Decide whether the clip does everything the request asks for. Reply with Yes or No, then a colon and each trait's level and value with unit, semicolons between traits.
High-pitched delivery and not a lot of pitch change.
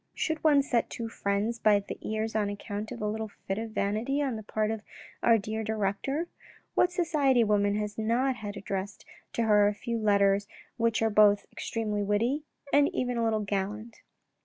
Yes: high, 220 Hz; narrow, 2.3 semitones